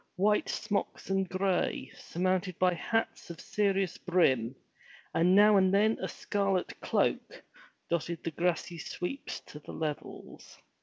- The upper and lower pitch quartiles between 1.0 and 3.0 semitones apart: Yes, narrow, 2.6 semitones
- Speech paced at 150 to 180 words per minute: No, slow, 135 wpm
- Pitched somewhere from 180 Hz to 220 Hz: Yes, medium, 185 Hz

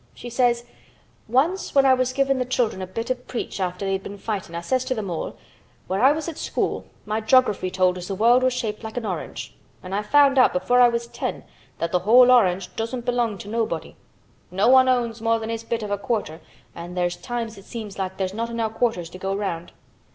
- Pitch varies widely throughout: No, average, 4.5 semitones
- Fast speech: Yes, fast, 230 wpm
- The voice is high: Yes, high, 225 Hz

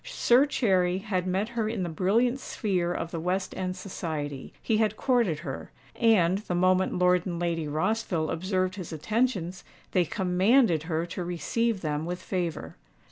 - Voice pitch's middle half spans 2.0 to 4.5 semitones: Yes, average, 4.0 semitones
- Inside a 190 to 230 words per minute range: No, average, 165 wpm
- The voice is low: No, medium, 185 Hz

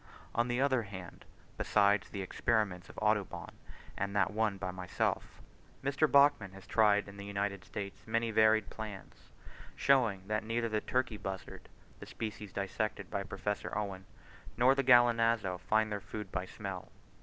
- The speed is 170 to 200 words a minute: No, average, 155 wpm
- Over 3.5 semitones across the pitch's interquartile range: No, average, 2.8 semitones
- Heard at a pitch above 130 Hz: No, low, 105 Hz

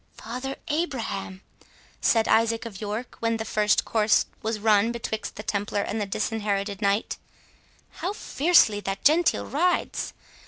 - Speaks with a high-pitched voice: Yes, high, 220 Hz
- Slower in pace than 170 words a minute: Yes, average, 140 wpm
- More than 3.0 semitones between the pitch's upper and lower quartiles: No, narrow, 2.4 semitones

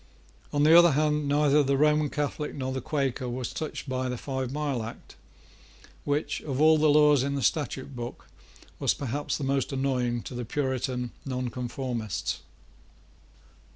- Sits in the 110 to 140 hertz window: Yes, low, 135 Hz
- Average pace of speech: Yes, average, 155 wpm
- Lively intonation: No, average, 2.7 semitones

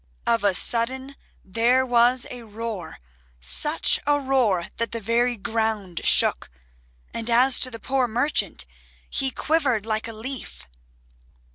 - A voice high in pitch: Yes, high, 230 Hz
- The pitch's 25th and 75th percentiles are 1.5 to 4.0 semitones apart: Yes, average, 3.0 semitones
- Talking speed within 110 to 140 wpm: Yes, slow, 135 wpm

